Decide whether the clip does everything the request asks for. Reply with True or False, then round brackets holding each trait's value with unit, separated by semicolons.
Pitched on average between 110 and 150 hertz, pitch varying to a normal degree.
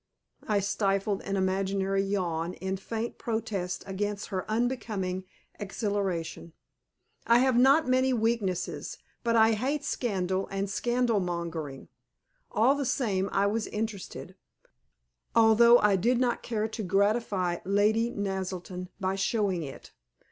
False (200 Hz; 3.3 semitones)